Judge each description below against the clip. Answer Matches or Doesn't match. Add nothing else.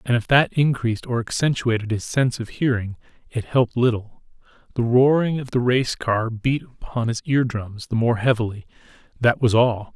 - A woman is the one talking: Doesn't match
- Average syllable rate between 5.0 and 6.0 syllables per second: Matches